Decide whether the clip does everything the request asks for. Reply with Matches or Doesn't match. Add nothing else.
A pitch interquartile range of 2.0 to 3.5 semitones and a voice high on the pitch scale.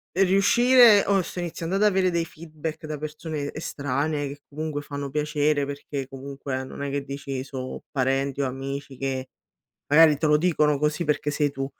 Doesn't match